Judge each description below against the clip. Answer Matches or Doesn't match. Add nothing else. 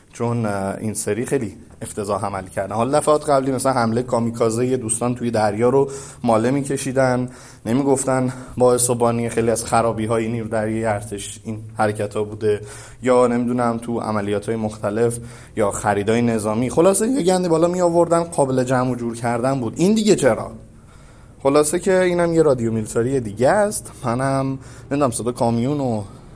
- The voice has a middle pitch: Doesn't match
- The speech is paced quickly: Matches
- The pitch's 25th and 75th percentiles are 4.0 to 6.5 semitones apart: Doesn't match